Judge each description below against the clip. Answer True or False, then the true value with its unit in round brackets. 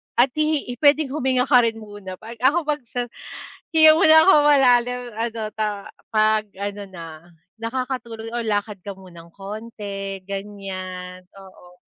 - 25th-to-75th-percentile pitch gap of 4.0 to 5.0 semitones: True (4.3 semitones)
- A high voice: True (220 Hz)